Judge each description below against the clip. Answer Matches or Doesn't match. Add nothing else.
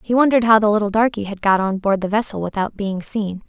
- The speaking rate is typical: Doesn't match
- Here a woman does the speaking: Matches